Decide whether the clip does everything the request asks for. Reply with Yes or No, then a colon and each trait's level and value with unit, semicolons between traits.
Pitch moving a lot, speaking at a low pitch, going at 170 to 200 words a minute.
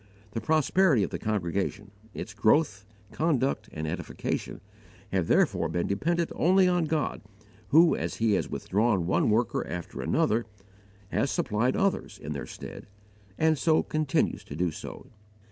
No: wide, 8.0 semitones; low, 115 Hz; average, 145 wpm